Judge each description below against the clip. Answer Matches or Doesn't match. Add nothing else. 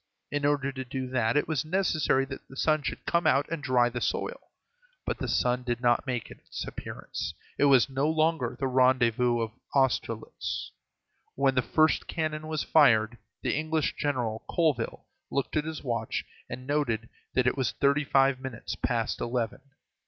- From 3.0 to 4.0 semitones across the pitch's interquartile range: Matches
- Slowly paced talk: Doesn't match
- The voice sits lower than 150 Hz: Matches